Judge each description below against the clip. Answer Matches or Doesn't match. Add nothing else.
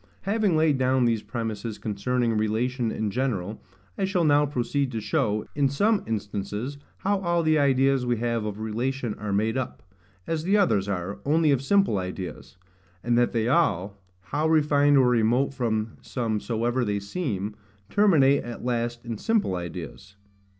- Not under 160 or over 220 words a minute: Matches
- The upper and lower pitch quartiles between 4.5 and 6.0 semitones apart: Matches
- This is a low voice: Matches